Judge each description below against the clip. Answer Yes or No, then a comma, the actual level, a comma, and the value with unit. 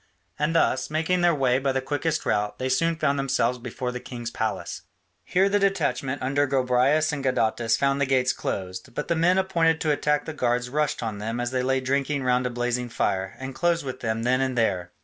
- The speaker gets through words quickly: Yes, fast, 215 wpm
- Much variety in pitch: No, average, 3.5 semitones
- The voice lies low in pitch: Yes, low, 130 Hz